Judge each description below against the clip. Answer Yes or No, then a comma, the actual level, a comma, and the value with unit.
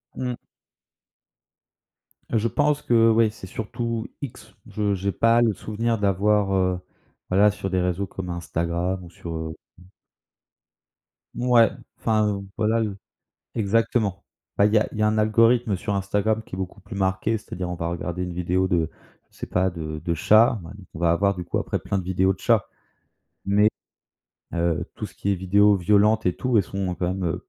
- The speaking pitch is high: No, low, 100 Hz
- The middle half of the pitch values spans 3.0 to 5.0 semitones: Yes, average, 3.4 semitones